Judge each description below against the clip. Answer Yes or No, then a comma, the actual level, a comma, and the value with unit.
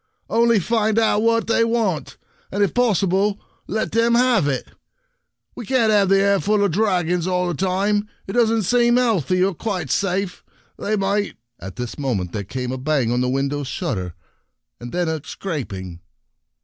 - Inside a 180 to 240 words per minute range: Yes, average, 185 wpm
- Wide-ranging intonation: Yes, wide, 7.2 semitones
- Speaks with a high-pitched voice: Yes, high, 195 Hz